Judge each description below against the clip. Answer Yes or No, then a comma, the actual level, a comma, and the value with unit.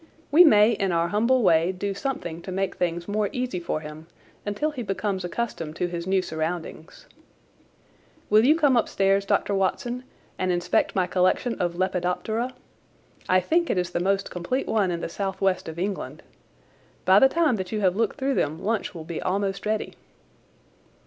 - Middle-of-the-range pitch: No, high, 195 Hz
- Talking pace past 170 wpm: Yes, average, 180 wpm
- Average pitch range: Yes, average, 3.9 semitones